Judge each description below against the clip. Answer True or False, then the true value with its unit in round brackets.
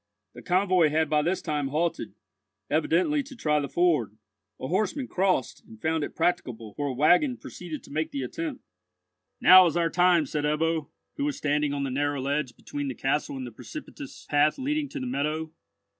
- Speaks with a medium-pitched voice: True (160 Hz)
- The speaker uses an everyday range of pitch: True (4.3 semitones)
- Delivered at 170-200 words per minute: True (190 wpm)